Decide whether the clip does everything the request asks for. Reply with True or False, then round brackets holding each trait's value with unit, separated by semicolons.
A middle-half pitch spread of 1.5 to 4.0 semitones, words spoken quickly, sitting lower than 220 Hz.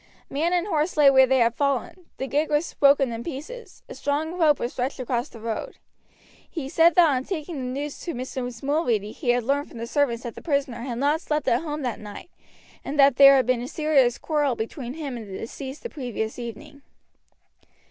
False (3.7 semitones; 215 wpm; 275 Hz)